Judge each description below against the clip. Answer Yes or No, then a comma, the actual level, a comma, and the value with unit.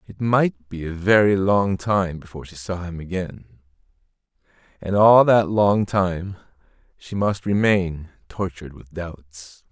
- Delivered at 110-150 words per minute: Yes, average, 140 wpm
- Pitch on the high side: No, very low, 95 Hz